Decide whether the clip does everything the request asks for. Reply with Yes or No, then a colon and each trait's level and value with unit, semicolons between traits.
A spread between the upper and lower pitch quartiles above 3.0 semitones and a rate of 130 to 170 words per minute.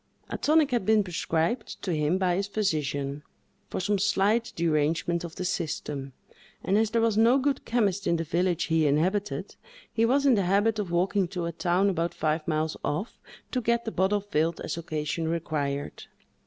No: average, 4.6 semitones; average, 185 wpm